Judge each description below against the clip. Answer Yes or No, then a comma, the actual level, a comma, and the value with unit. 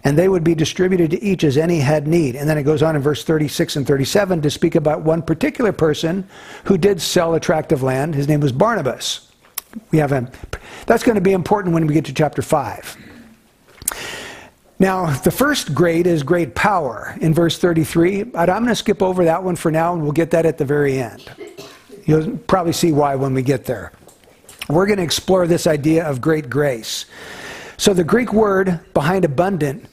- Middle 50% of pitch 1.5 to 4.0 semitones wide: Yes, average, 3.7 semitones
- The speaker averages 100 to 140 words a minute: No, fast, 205 wpm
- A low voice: No, medium, 165 Hz